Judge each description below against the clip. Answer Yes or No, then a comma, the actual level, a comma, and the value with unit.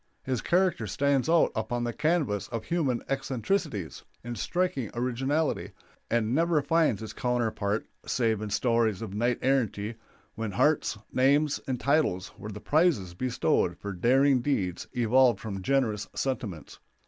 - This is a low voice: Yes, low, 120 Hz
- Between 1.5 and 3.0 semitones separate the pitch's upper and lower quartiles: No, average, 4.6 semitones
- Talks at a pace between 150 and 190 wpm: No, average, 140 wpm